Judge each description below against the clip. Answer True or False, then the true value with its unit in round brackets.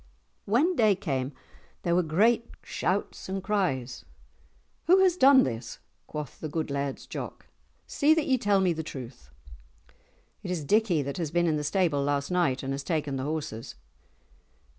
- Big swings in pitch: True (6.5 semitones)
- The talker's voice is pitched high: False (165 Hz)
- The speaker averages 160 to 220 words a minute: True (165 wpm)